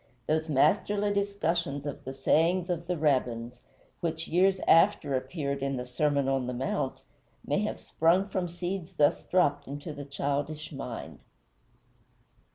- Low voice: No, medium, 155 Hz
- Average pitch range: Yes, average, 4.3 semitones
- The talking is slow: No, average, 145 wpm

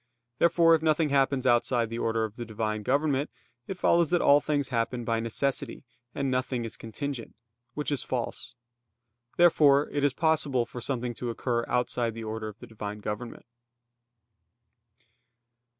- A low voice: Yes, low, 125 Hz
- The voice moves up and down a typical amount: Yes, average, 3.9 semitones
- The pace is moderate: Yes, average, 155 wpm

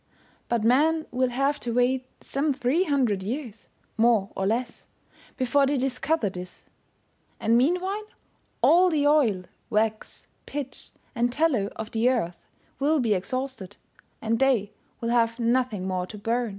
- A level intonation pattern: No, average, 4.0 semitones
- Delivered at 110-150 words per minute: Yes, average, 145 wpm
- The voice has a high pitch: Yes, high, 245 Hz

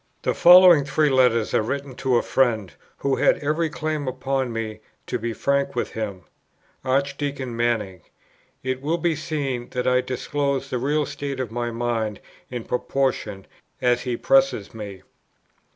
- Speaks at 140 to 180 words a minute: Yes, average, 155 wpm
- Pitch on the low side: Yes, low, 130 Hz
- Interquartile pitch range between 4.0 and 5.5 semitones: No, average, 3.2 semitones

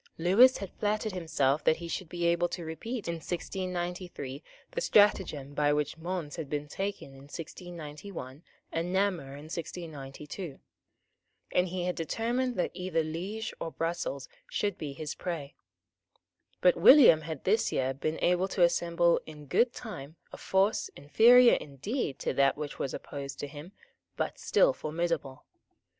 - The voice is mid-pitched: Yes, medium, 170 Hz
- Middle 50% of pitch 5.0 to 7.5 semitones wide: No, average, 4.4 semitones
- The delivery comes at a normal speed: Yes, average, 150 wpm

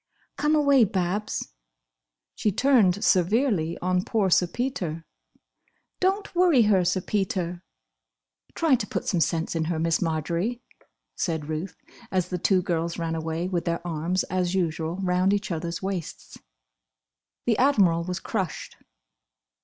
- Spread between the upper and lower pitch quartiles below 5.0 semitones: Yes, average, 3.9 semitones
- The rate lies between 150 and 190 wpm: No, average, 140 wpm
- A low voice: No, medium, 180 Hz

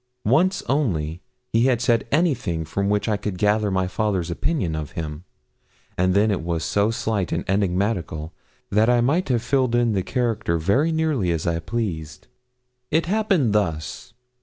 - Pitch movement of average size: No, wide, 5.7 semitones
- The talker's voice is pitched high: No, low, 105 Hz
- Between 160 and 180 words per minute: Yes, average, 165 wpm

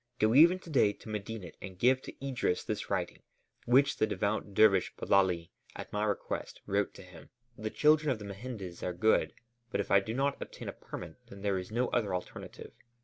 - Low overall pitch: Yes, low, 105 Hz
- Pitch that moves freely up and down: No, average, 4.1 semitones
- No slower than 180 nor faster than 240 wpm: Yes, average, 200 wpm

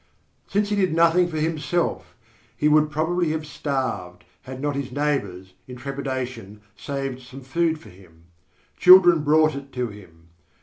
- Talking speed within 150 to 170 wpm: Yes, average, 155 wpm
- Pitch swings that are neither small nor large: Yes, average, 4.3 semitones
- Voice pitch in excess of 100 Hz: Yes, medium, 140 Hz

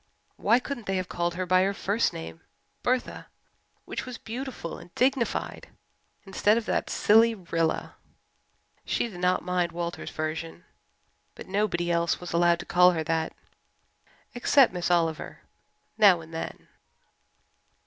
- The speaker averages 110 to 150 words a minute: Yes, average, 140 wpm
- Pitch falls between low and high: Yes, medium, 180 Hz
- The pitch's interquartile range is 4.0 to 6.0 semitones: Yes, average, 4.4 semitones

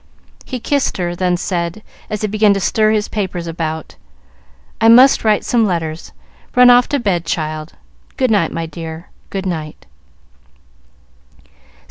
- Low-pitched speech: No, high, 190 Hz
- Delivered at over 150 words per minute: No, average, 145 wpm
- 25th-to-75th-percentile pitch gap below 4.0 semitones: No, average, 4.7 semitones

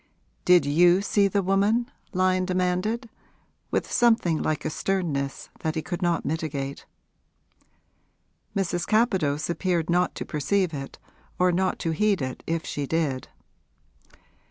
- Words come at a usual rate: No, slow, 130 wpm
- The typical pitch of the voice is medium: Yes, medium, 180 Hz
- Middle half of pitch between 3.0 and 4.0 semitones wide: Yes, average, 3.7 semitones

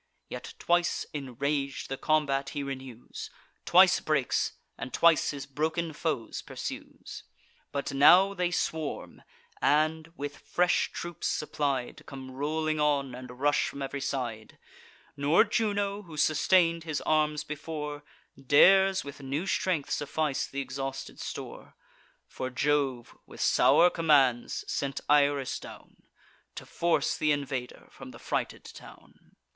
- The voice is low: No, medium, 145 Hz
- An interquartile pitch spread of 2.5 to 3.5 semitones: Yes, average, 2.8 semitones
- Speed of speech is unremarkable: No, slow, 130 wpm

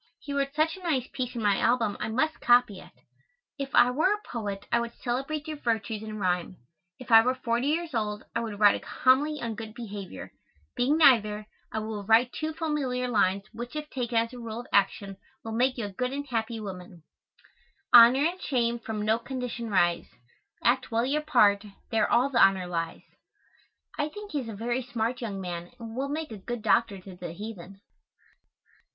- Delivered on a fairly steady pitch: No, average, 3.9 semitones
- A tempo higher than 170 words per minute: Yes, average, 200 wpm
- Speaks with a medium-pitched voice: No, high, 235 Hz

